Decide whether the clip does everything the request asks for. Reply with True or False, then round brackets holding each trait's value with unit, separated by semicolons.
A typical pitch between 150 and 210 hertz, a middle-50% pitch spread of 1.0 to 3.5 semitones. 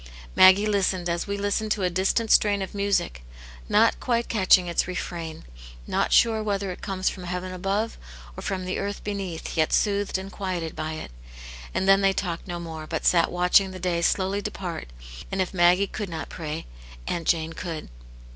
True (185 Hz; 2.6 semitones)